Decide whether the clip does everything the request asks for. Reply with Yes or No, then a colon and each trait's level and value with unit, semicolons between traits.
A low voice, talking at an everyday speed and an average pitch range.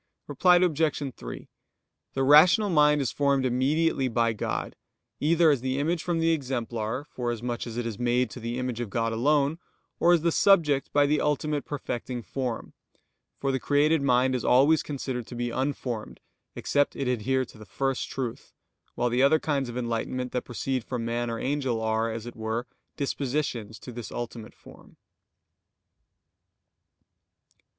Yes: low, 130 Hz; average, 165 wpm; average, 3.5 semitones